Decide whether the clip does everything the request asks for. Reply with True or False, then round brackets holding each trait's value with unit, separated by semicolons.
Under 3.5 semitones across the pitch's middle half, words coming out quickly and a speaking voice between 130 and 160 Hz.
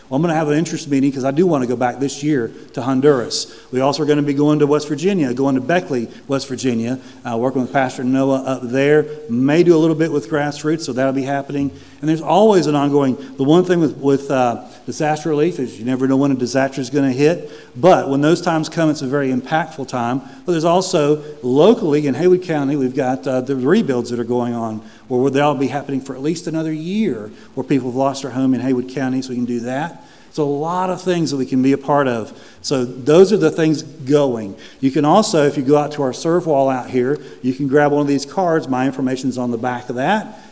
True (2.7 semitones; 255 wpm; 140 Hz)